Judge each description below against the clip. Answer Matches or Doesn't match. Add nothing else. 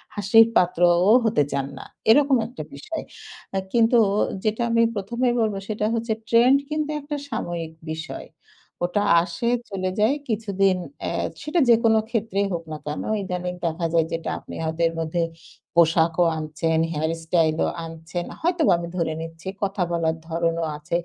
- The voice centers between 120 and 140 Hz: Doesn't match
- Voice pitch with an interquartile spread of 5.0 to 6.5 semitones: Matches